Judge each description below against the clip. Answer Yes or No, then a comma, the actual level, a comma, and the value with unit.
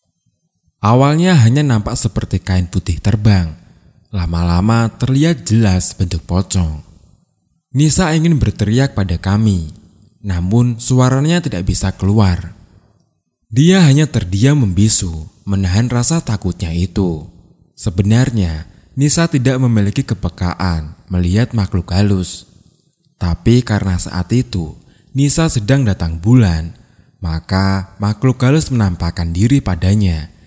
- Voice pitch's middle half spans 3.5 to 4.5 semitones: No, wide, 5.6 semitones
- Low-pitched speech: Yes, low, 105 Hz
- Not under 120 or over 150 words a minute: No, average, 100 wpm